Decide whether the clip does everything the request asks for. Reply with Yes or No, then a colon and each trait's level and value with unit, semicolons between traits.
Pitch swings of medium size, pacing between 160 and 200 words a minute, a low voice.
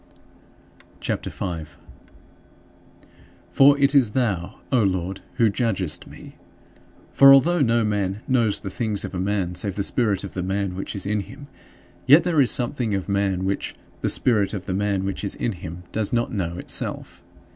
Yes: average, 4.2 semitones; average, 180 wpm; low, 100 Hz